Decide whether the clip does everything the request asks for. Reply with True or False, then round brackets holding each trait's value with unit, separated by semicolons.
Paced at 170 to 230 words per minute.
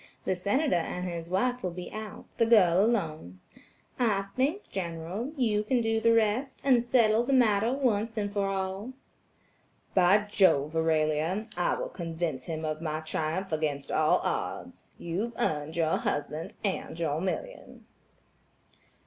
False (145 wpm)